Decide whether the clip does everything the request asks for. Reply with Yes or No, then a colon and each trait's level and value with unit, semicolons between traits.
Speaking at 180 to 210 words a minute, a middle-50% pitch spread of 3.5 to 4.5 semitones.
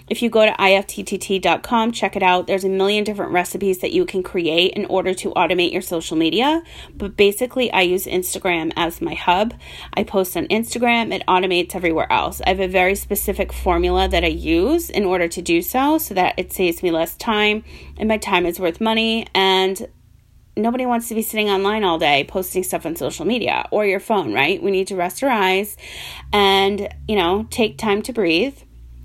No: average, 200 wpm; average, 2.8 semitones